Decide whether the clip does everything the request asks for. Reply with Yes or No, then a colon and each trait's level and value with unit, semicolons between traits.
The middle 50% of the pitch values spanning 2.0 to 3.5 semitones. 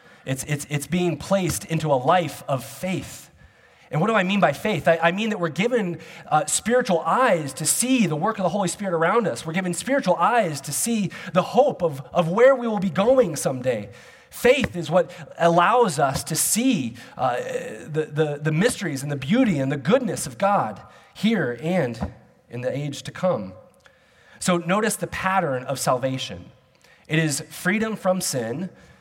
No: average, 5.2 semitones